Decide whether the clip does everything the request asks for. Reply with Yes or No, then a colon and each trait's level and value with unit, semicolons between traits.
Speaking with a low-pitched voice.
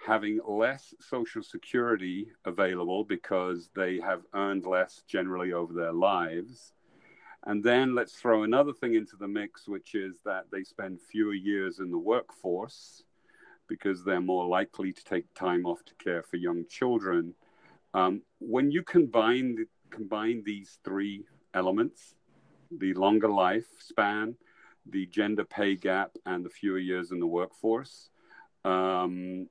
Yes: very low, 95 Hz